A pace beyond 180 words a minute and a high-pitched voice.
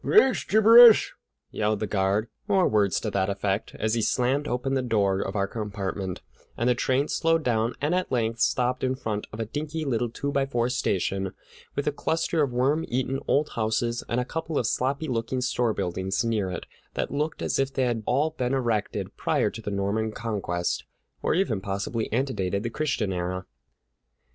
No: average, 190 wpm; low, 120 Hz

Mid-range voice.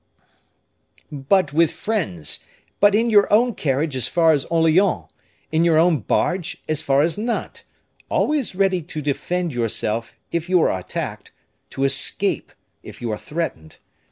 Yes: medium, 160 Hz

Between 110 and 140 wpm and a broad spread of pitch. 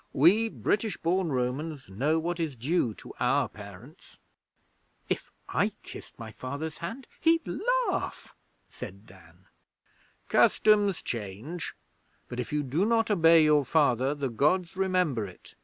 Yes: slow, 135 wpm; wide, 6.4 semitones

